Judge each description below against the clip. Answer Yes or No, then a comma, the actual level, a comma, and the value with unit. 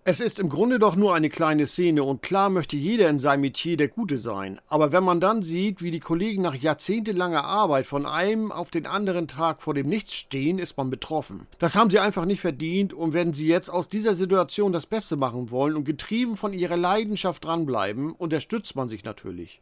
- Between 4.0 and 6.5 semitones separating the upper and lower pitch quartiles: Yes, average, 4.8 semitones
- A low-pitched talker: No, medium, 170 Hz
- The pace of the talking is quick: Yes, fast, 215 wpm